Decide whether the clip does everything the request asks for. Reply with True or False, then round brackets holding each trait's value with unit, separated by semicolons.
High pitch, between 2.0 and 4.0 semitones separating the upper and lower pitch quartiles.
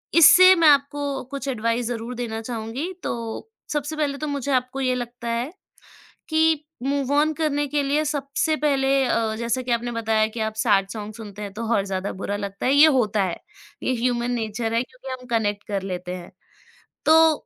False (245 Hz; 4.5 semitones)